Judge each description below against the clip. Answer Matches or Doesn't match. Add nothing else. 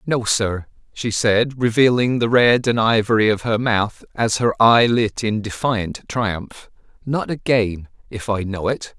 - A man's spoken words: Matches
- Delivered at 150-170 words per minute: Matches